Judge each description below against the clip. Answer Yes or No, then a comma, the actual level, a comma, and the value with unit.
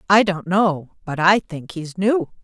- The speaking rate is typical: Yes, average, 195 wpm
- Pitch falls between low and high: Yes, medium, 180 Hz